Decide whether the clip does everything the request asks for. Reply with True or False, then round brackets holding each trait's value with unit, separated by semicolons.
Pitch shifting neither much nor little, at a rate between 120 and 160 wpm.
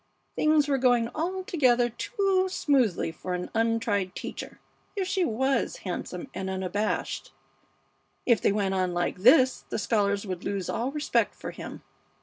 False (7.1 semitones; 145 wpm)